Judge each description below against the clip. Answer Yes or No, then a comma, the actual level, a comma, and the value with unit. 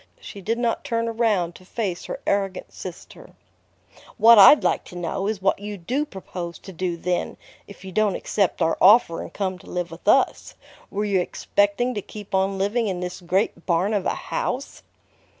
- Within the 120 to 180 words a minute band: No, average, 190 wpm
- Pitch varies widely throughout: No, average, 3.4 semitones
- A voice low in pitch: No, high, 195 Hz